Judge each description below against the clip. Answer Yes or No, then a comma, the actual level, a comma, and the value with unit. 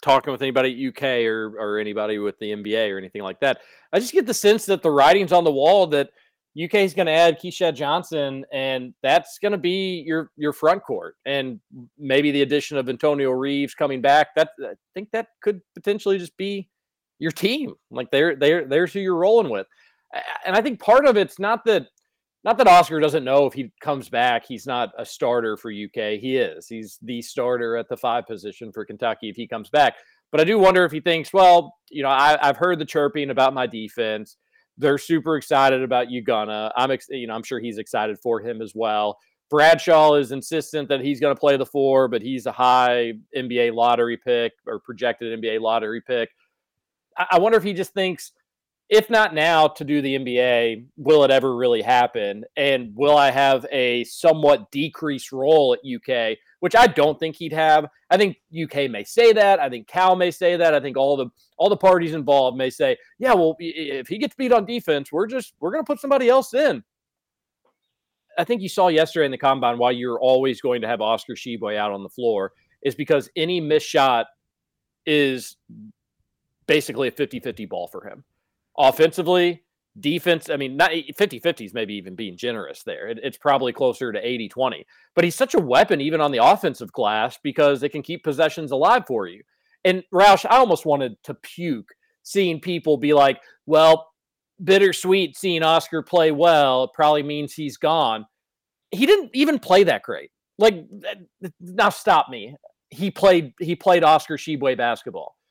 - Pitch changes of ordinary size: No, wide, 6.3 semitones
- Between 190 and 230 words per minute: Yes, average, 195 wpm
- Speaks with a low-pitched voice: No, medium, 150 Hz